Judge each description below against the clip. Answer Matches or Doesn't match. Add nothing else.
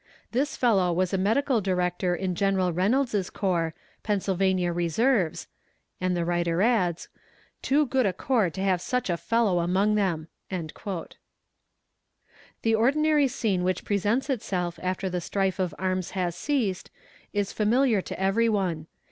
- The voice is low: Doesn't match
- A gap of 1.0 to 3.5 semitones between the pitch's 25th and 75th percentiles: Doesn't match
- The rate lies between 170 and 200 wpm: Doesn't match